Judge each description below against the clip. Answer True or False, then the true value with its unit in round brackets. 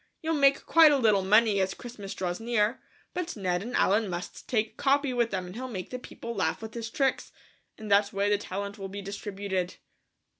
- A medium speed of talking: False (210 wpm)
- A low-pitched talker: False (210 Hz)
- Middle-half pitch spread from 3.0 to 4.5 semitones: True (3.9 semitones)